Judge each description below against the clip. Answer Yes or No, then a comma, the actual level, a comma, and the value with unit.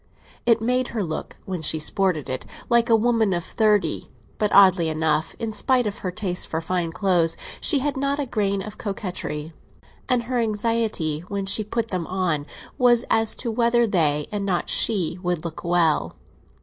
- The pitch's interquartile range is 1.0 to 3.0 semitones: No, average, 5.1 semitones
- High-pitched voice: Yes, high, 200 Hz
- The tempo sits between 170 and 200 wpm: Yes, average, 180 wpm